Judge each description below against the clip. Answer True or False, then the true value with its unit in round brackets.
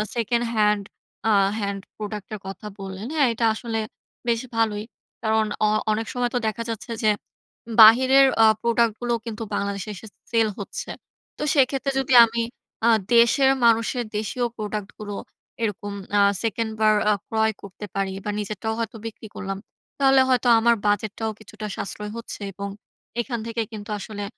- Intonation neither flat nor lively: False (2.1 semitones)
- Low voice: False (220 Hz)